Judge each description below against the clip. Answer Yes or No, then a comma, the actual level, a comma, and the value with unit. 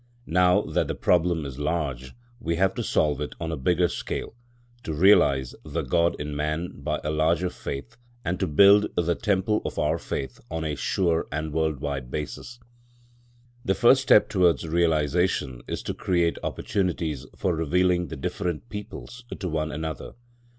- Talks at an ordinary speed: Yes, average, 165 wpm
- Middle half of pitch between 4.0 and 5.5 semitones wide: No, average, 3.3 semitones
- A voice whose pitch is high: No, very low, 80 Hz